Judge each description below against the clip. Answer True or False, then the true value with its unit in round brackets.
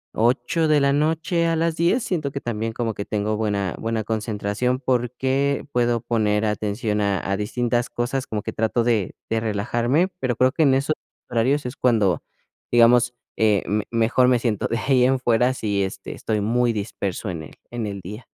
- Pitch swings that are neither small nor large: True (3.4 semitones)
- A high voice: False (120 Hz)